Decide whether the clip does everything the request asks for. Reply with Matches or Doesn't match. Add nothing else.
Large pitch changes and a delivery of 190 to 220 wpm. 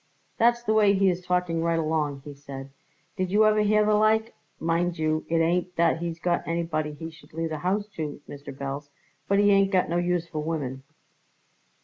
Doesn't match